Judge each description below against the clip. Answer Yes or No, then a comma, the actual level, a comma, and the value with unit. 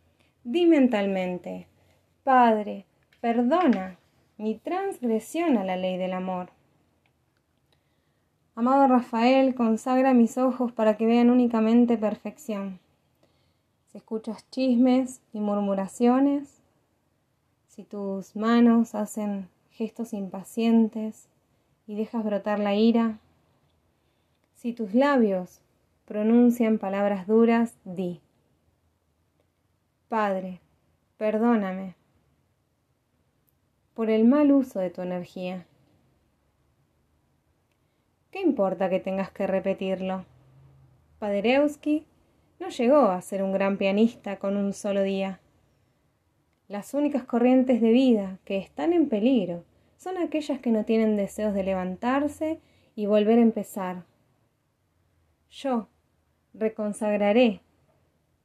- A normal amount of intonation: Yes, average, 4.2 semitones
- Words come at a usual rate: No, slow, 95 wpm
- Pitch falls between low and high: No, high, 210 Hz